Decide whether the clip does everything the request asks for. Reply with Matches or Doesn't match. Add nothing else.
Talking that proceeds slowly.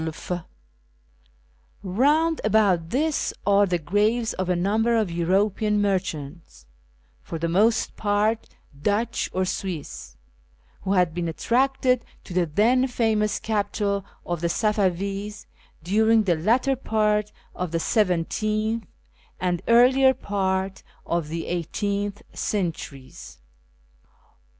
Matches